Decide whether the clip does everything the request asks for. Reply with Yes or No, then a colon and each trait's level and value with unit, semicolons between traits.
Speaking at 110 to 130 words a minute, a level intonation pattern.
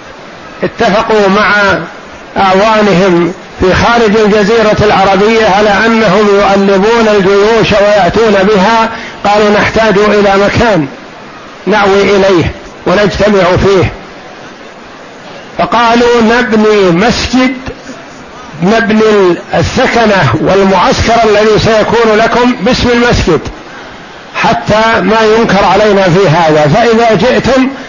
No: average, 85 wpm; narrow, 2.3 semitones